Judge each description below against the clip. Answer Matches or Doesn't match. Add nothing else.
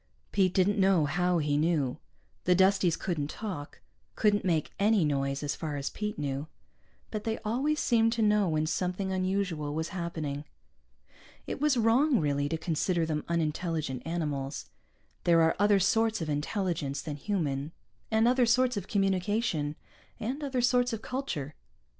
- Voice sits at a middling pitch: Matches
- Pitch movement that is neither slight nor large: Doesn't match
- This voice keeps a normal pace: Matches